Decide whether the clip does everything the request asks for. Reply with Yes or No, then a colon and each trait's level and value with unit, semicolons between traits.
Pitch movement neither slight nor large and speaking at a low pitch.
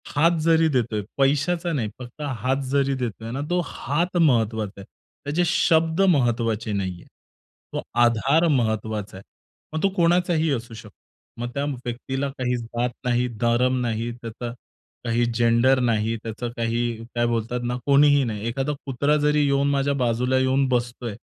Yes: average, 3.6 semitones; low, 125 Hz